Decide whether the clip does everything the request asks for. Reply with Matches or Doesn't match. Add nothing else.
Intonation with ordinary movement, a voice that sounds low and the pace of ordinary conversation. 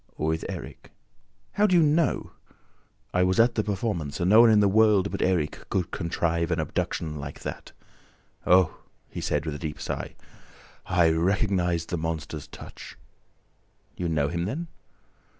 Matches